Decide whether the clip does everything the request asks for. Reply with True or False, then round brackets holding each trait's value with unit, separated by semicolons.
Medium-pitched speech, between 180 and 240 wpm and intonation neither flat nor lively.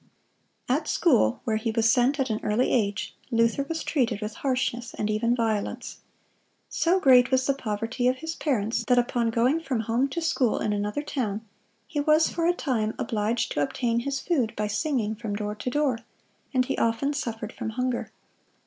False (240 Hz; 185 wpm; 3.8 semitones)